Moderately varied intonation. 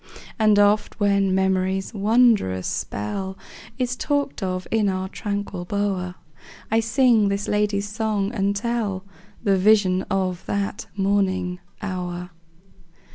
No: narrow, 2.2 semitones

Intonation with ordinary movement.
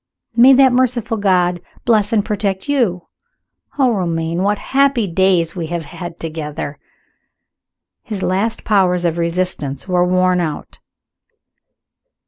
Yes: average, 4.4 semitones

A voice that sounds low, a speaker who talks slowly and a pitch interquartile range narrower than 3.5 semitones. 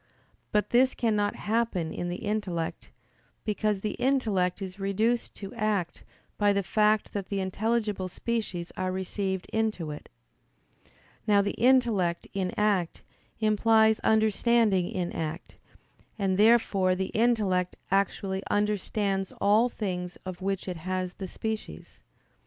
No: high, 200 Hz; slow, 130 wpm; average, 2.8 semitones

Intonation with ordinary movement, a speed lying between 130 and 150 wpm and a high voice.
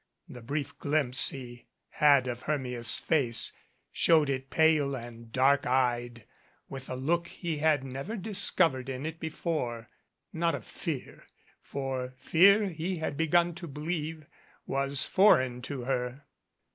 No: average, 3.9 semitones; average, 140 wpm; medium, 140 Hz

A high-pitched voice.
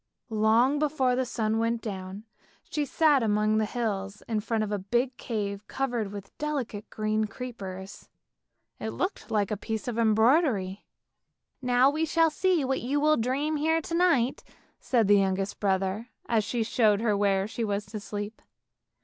Yes: high, 220 Hz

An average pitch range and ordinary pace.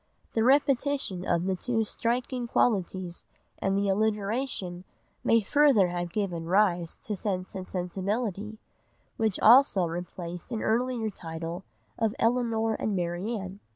No: average, 4.2 semitones; slow, 120 wpm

